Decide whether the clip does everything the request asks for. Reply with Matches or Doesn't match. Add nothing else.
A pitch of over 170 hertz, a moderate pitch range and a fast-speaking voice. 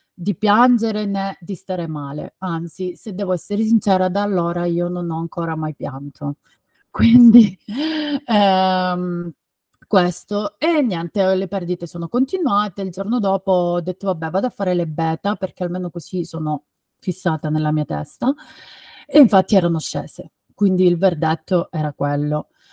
Doesn't match